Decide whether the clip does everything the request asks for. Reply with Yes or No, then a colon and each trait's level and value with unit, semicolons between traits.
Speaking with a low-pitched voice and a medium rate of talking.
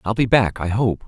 No: low, 105 Hz; fast, 225 wpm